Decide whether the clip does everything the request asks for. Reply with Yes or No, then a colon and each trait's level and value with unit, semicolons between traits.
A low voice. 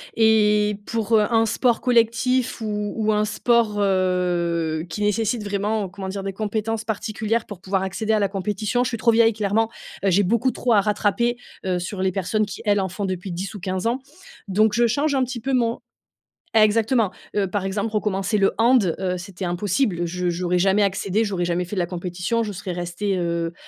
No: high, 205 Hz